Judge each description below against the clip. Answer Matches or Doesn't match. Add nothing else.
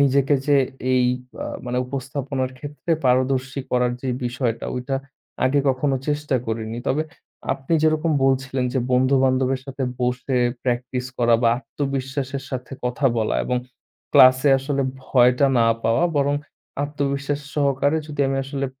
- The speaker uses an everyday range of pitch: Doesn't match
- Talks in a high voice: Doesn't match